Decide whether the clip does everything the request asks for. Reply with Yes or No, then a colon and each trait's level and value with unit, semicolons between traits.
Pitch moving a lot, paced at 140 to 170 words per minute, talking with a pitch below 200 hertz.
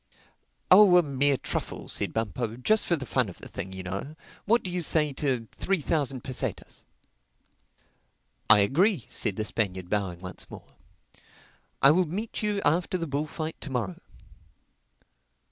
Yes: wide, 8.2 semitones; average, 150 wpm; medium, 140 Hz